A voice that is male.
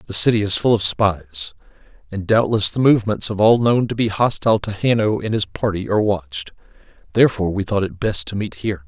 Yes: male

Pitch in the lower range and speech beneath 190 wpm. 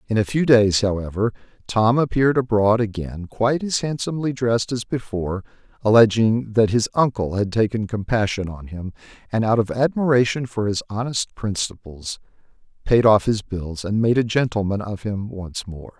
Yes: low, 110 Hz; average, 165 wpm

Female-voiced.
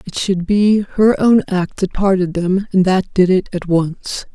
Yes: female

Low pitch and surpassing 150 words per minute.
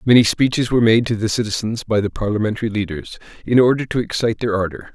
Yes: low, 110 Hz; fast, 205 wpm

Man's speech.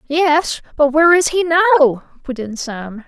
No: female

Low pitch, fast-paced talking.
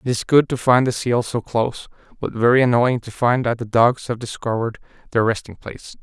Yes: low, 120 Hz; fast, 220 wpm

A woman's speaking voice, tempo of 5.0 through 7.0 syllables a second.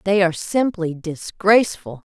No: female; 4.7 syllables/s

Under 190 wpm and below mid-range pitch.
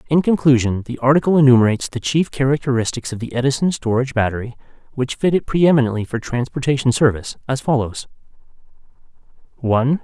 Yes: average, 140 wpm; low, 130 Hz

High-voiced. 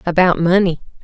No: medium, 175 Hz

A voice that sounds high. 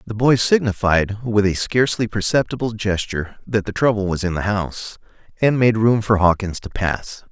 No: low, 105 Hz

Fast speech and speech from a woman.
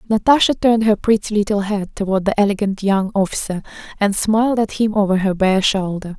No: average, 185 wpm; female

